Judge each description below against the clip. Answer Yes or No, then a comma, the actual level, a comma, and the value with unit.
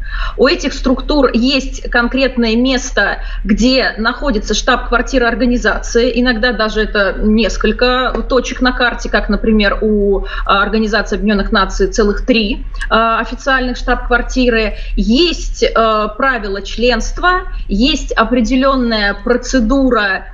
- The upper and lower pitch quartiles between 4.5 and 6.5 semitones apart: No, average, 2.8 semitones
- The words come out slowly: Yes, slow, 95 wpm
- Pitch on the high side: Yes, high, 240 Hz